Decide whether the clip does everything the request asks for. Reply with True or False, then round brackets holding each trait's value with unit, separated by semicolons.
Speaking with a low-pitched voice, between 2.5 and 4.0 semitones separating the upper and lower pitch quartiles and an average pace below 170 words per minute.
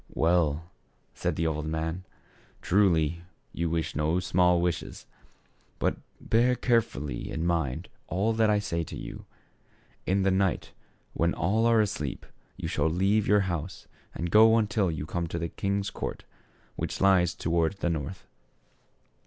True (90 Hz; 3.4 semitones; 150 wpm)